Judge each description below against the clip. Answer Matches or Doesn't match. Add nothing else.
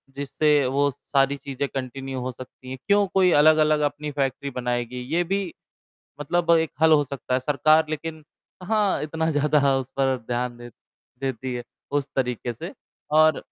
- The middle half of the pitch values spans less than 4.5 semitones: Matches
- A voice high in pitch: Doesn't match